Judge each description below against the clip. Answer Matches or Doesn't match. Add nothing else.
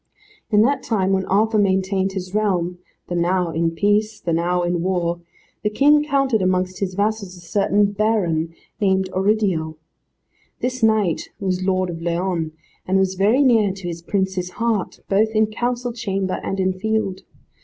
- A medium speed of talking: Matches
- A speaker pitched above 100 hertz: Matches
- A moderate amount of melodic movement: Matches